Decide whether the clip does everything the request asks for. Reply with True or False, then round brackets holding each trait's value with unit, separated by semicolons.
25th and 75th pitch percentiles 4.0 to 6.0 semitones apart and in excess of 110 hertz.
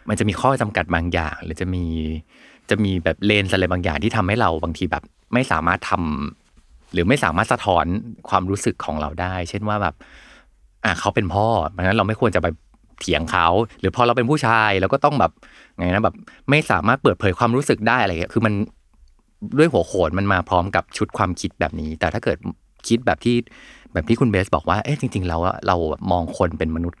False (4.7 semitones; 95 Hz)